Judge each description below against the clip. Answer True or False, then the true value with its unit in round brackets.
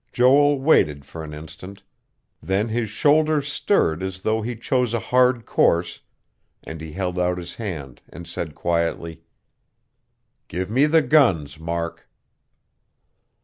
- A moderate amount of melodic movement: False (7.1 semitones)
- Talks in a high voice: False (95 Hz)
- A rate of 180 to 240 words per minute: False (135 wpm)